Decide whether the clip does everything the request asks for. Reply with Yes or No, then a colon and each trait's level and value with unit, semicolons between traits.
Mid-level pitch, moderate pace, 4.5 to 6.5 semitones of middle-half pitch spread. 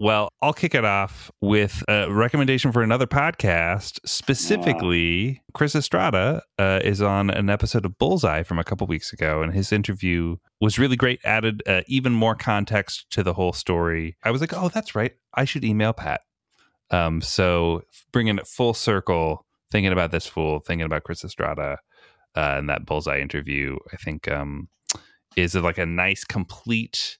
No: low, 100 Hz; average, 170 wpm; average, 5.1 semitones